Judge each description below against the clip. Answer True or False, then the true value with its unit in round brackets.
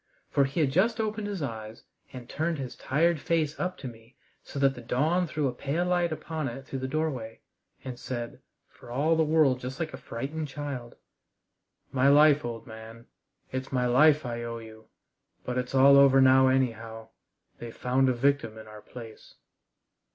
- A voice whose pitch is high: False (135 Hz)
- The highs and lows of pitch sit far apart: False (4.3 semitones)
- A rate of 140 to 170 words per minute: False (180 wpm)